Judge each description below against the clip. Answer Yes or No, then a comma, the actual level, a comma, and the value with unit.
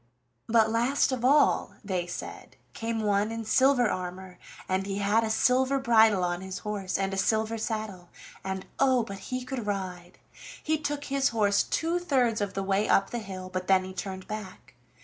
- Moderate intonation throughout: Yes, average, 4.2 semitones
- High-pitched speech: Yes, high, 210 Hz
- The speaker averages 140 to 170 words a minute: No, average, 190 wpm